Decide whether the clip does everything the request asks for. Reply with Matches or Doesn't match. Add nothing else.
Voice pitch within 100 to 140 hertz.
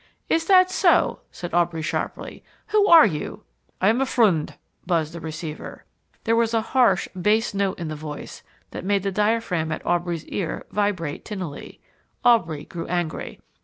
Doesn't match